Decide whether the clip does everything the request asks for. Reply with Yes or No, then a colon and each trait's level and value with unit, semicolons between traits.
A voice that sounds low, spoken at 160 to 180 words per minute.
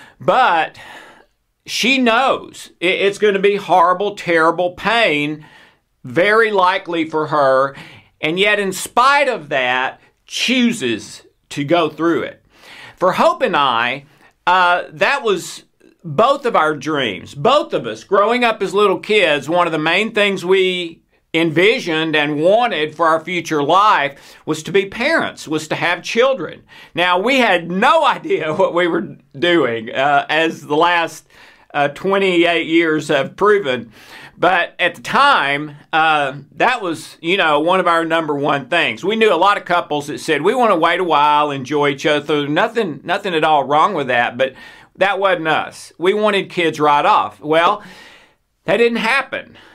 No: medium, 170 Hz; average, 165 wpm